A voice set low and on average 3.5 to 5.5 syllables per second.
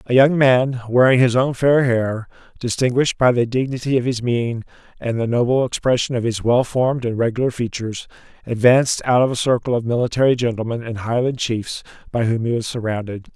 No: low, 120 Hz; 5.7 syllables/s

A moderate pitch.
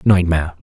No: very low, 85 Hz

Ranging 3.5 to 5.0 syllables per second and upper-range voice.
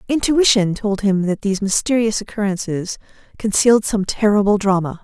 No: 5.4 syllables/s; high, 205 Hz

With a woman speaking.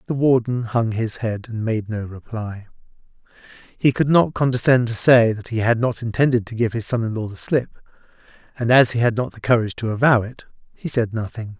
No: male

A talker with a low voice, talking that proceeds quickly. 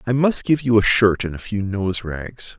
Yes: low, 105 Hz; fast, 230 wpm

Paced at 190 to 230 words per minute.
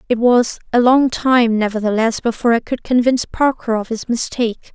No: average, 175 wpm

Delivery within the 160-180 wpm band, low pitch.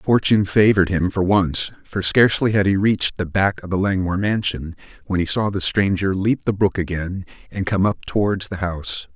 No: fast, 205 wpm; very low, 95 Hz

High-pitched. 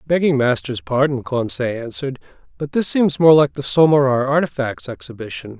No: medium, 140 Hz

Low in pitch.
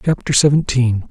Yes: low, 130 Hz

